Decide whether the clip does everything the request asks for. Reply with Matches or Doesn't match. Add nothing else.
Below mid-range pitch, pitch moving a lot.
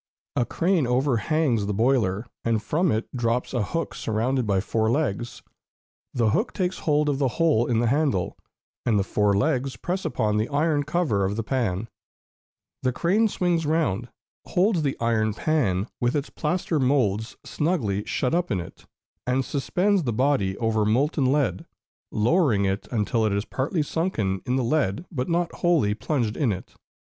Matches